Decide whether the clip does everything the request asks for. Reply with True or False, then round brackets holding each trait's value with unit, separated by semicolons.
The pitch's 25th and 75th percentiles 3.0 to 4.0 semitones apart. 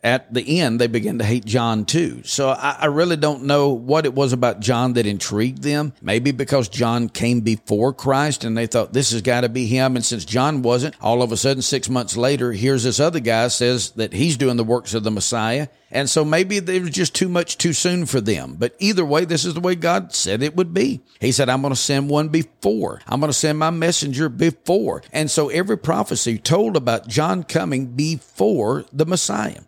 False (4.7 semitones)